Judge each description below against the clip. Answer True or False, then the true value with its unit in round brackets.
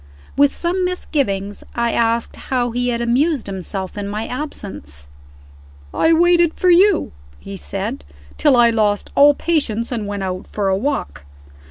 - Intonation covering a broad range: True (6.7 semitones)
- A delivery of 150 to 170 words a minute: True (155 wpm)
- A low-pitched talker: False (235 Hz)